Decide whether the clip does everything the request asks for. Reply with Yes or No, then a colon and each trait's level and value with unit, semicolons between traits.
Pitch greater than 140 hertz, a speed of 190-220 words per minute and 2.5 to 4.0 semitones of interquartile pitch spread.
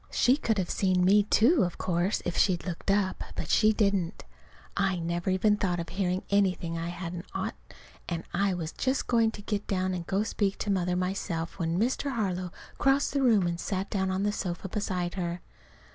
Yes: high, 190 Hz; fast, 205 wpm; average, 2.8 semitones